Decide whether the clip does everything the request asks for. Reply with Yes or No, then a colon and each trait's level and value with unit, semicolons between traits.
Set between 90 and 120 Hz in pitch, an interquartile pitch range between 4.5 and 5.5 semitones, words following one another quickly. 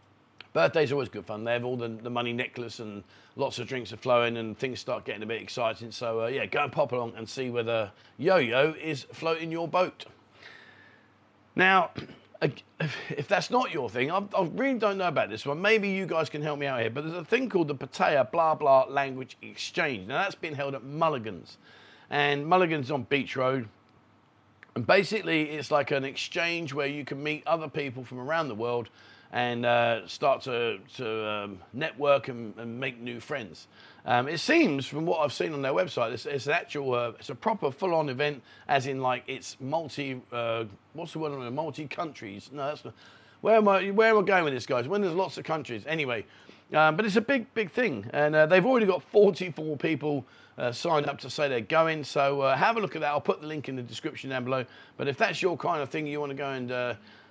No: medium, 140 Hz; average, 5.1 semitones; fast, 225 wpm